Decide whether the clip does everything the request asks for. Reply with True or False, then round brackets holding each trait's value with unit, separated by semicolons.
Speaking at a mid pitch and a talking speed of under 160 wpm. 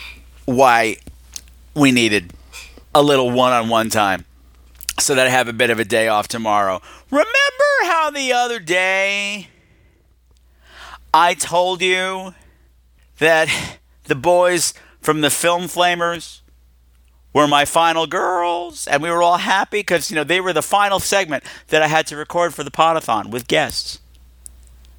True (145 Hz; 150 wpm)